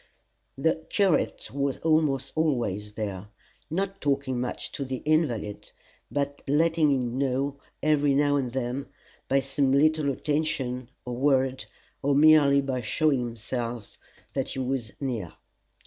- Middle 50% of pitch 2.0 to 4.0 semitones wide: Yes, average, 2.9 semitones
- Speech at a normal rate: No, slow, 130 wpm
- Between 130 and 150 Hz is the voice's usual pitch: Yes, low, 135 Hz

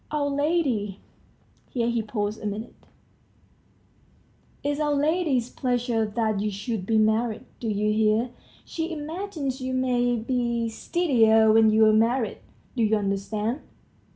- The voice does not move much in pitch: No, average, 3.6 semitones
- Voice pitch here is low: No, high, 235 Hz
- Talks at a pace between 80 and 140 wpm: Yes, slow, 135 wpm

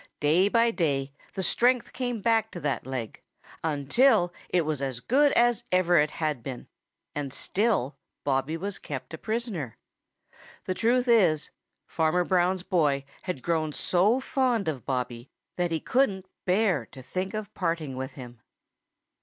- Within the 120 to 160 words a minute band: Yes, average, 155 wpm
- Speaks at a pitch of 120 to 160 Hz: No, medium, 175 Hz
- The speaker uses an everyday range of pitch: No, wide, 7.2 semitones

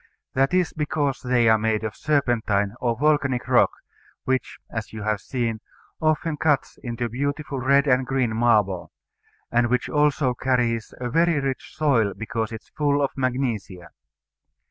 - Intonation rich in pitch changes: No, average, 4.1 semitones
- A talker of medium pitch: No, low, 125 Hz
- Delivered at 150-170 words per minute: Yes, average, 155 wpm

